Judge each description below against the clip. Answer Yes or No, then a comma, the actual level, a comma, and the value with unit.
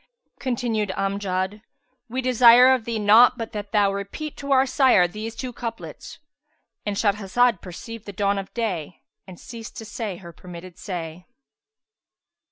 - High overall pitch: Yes, high, 210 Hz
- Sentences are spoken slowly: No, average, 150 wpm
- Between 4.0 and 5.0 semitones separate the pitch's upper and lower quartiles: No, average, 3.6 semitones